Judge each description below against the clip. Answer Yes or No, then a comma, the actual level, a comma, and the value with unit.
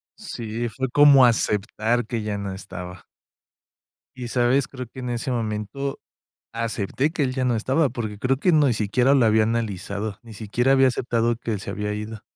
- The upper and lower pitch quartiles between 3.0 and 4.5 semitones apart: Yes, average, 3.3 semitones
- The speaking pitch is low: Yes, low, 115 Hz